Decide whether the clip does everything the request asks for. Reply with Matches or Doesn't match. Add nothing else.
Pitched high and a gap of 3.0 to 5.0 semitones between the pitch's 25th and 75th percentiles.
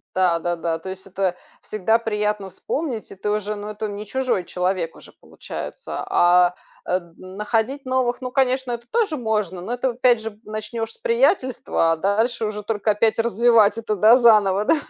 Matches